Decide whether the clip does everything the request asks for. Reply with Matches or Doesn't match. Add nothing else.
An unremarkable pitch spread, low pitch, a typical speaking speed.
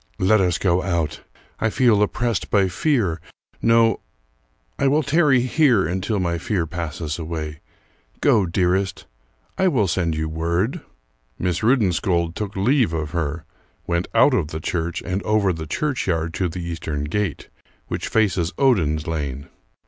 Matches